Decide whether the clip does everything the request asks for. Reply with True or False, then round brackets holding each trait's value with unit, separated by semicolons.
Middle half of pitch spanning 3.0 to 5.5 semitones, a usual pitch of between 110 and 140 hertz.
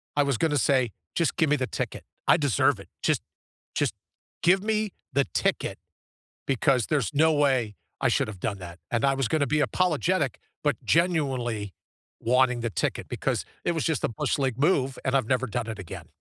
True (4.5 semitones; 135 Hz)